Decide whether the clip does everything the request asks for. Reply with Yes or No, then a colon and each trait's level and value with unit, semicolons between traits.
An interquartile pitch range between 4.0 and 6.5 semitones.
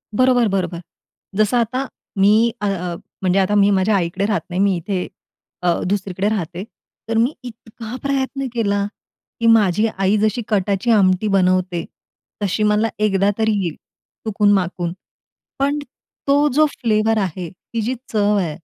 No: average, 3.2 semitones